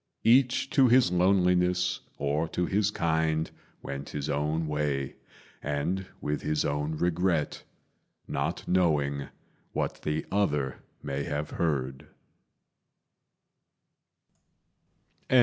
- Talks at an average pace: No, slow, 95 wpm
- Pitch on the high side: No, very low, 80 Hz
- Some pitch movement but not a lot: Yes, average, 3.8 semitones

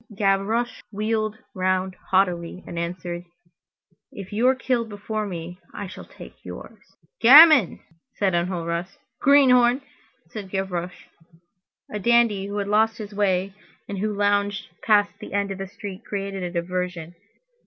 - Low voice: No, high, 200 Hz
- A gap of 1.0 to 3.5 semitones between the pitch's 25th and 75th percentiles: Yes, average, 2.8 semitones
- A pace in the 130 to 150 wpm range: Yes, average, 140 wpm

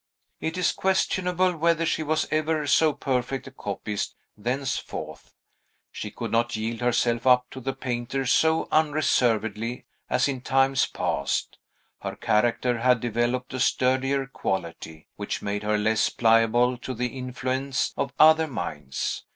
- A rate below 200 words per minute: Yes, average, 140 wpm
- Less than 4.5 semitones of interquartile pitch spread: Yes, average, 3.2 semitones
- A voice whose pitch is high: No, low, 125 Hz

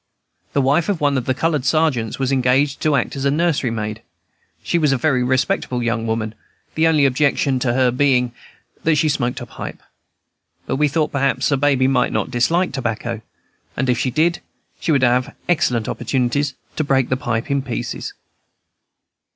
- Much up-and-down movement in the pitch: No, average, 3.0 semitones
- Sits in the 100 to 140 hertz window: Yes, low, 135 Hz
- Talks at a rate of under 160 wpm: No, average, 180 wpm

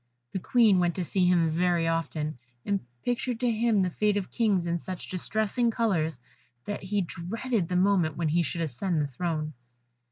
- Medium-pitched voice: Yes, medium, 180 Hz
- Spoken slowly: No, average, 185 wpm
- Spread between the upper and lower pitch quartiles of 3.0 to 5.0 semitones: Yes, average, 4.1 semitones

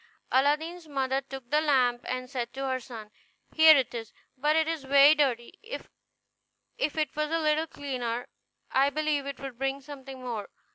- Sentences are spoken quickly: No, average, 175 wpm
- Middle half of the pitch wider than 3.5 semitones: No, average, 3.1 semitones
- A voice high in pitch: Yes, very high, 275 Hz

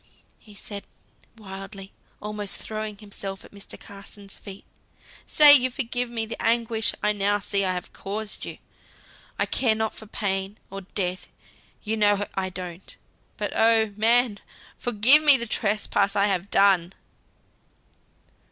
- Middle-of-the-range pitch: No, high, 205 Hz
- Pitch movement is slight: Yes, narrow, 2.2 semitones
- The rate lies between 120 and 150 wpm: Yes, average, 145 wpm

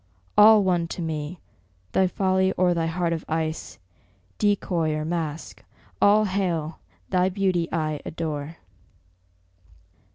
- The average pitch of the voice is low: No, medium, 170 Hz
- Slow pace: Yes, slow, 120 wpm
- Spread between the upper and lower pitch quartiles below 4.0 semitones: Yes, average, 2.9 semitones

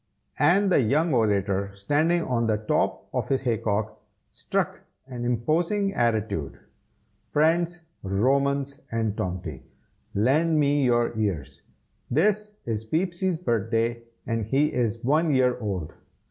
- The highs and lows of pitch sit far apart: Yes, wide, 6.1 semitones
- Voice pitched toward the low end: Yes, low, 125 Hz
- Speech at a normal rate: No, slow, 125 wpm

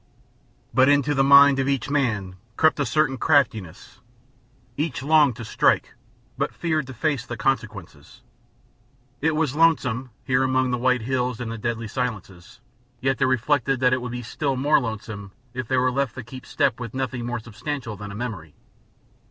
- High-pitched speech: No, low, 130 Hz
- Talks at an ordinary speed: Yes, average, 175 wpm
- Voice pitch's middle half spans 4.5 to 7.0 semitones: No, average, 3.3 semitones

